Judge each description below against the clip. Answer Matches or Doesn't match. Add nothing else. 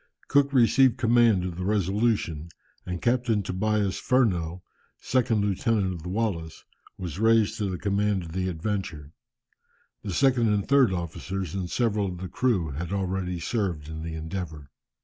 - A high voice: Doesn't match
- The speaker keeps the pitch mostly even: Doesn't match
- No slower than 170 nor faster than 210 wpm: Doesn't match